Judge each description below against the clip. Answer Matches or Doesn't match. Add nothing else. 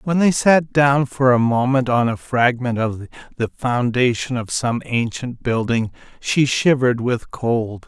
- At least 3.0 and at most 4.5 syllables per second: Matches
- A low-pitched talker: Matches